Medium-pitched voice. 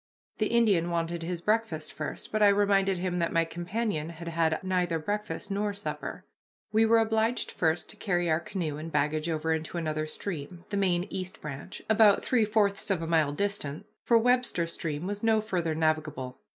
Yes: medium, 175 Hz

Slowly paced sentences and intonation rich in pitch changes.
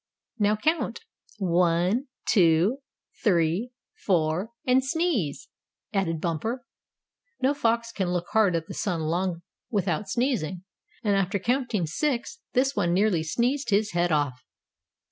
Yes: slow, 125 wpm; wide, 5.9 semitones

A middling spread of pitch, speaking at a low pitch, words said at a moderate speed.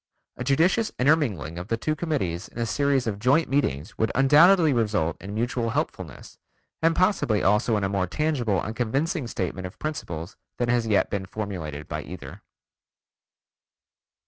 No: wide, 6.9 semitones; low, 115 Hz; average, 160 wpm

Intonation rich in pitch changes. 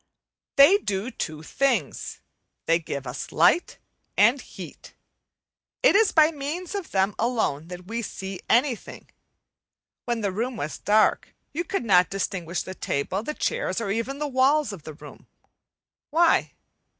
Yes: wide, 7.9 semitones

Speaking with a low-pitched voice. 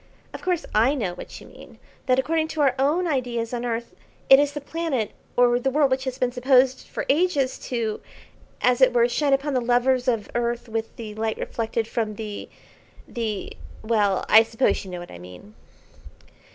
No: high, 245 Hz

